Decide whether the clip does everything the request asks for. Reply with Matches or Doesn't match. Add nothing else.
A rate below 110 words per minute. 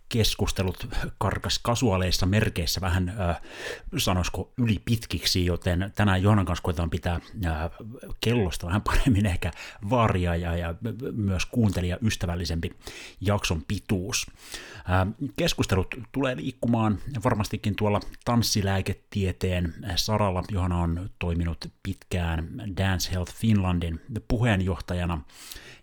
Matches